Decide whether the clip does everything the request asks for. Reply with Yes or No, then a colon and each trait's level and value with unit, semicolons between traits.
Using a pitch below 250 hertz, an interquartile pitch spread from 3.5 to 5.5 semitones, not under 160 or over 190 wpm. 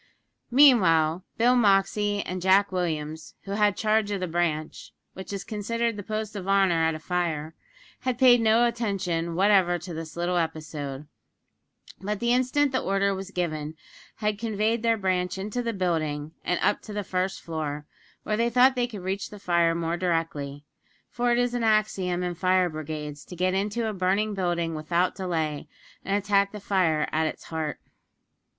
Yes: high, 190 Hz; average, 4.3 semitones; average, 175 wpm